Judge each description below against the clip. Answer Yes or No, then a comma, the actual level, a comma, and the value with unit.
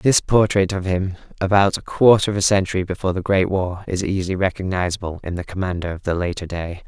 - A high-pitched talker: No, very low, 95 Hz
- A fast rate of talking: Yes, fast, 210 wpm